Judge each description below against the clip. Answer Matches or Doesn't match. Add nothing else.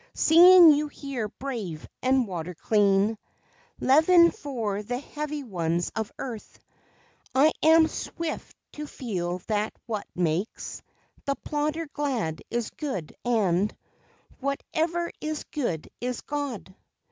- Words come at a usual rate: Doesn't match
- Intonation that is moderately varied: Doesn't match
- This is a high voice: Matches